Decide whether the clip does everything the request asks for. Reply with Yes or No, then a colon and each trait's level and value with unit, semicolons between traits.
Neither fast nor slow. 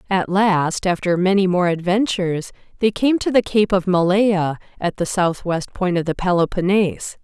Yes: average, 165 wpm